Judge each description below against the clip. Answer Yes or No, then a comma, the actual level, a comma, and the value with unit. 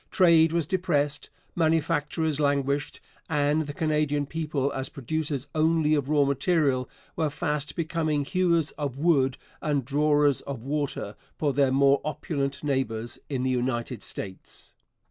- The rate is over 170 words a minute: No, slow, 135 wpm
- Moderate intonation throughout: No, narrow, 2.3 semitones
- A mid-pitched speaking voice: Yes, medium, 145 Hz